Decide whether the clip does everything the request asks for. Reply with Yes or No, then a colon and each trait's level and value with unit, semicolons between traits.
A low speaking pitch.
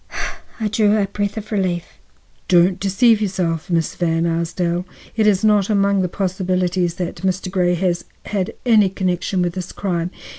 No: medium, 185 Hz